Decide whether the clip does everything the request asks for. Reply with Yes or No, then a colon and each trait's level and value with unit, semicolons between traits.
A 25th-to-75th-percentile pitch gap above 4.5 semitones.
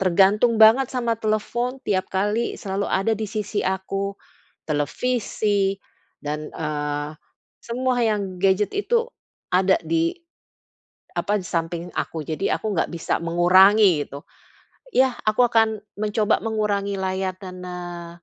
No: average, 3.4 semitones